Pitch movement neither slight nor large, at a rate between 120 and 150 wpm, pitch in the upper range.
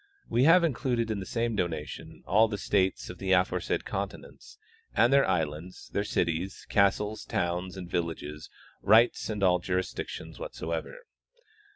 No: average, 4.1 semitones; average, 140 wpm; very low, 95 Hz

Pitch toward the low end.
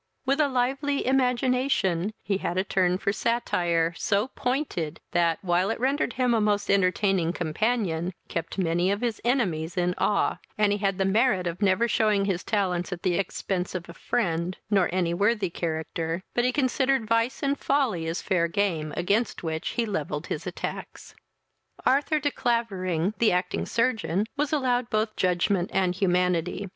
No: high, 195 Hz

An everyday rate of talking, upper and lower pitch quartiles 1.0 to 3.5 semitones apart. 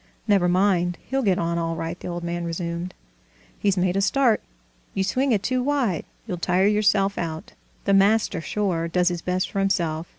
Yes: average, 190 wpm; average, 3.0 semitones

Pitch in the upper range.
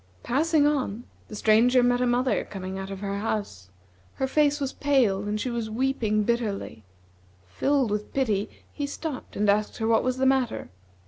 Yes: high, 235 Hz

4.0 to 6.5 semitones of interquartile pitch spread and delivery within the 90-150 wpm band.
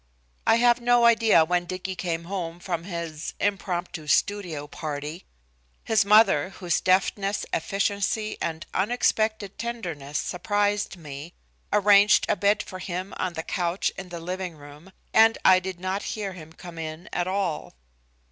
No: average, 3.5 semitones; average, 145 wpm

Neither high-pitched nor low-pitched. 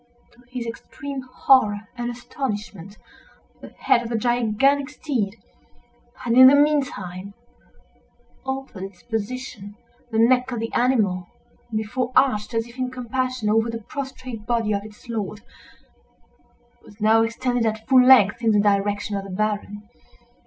No: high, 230 Hz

